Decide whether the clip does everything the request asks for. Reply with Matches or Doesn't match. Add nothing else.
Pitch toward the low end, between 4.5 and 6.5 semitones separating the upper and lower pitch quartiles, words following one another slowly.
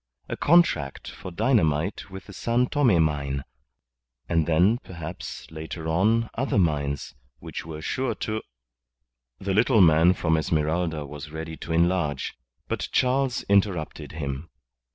Matches